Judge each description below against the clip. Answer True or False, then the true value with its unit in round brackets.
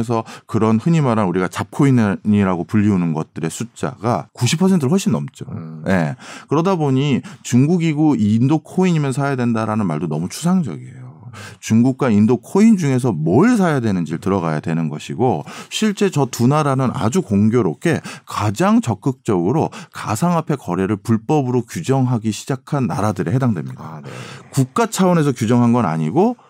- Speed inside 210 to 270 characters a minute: False (345 characters per minute)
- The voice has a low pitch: True (125 Hz)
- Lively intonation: True (6.5 semitones)